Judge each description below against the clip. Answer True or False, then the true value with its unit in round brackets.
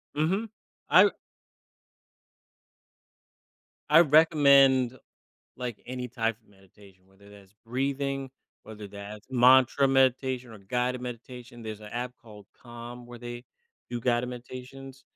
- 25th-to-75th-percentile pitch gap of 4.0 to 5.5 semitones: False (3.1 semitones)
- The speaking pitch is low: True (125 Hz)